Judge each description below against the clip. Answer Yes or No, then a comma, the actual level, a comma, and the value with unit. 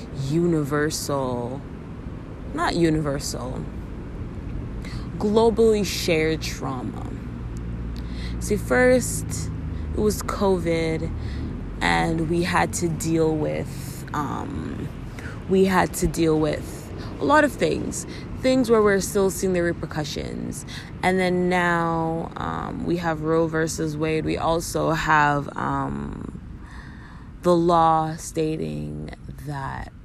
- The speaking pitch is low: No, medium, 160 Hz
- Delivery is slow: Yes, slow, 100 wpm